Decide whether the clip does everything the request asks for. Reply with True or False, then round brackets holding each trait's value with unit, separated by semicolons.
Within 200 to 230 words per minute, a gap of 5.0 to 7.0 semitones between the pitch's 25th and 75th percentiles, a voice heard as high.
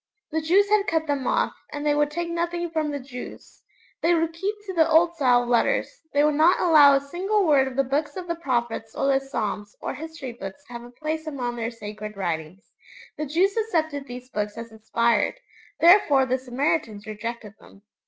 True (205 wpm; 5.4 semitones; 285 Hz)